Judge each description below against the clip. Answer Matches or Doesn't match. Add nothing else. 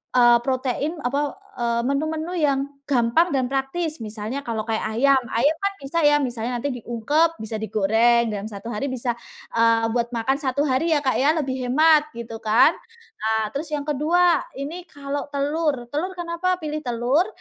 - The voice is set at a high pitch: Matches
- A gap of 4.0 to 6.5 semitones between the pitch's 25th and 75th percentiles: Matches